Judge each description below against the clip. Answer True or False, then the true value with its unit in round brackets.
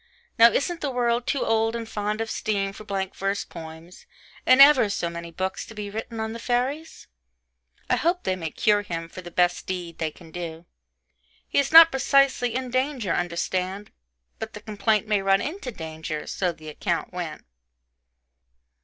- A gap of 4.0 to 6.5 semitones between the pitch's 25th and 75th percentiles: True (5.6 semitones)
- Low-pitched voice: False (210 Hz)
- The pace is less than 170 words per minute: False (180 wpm)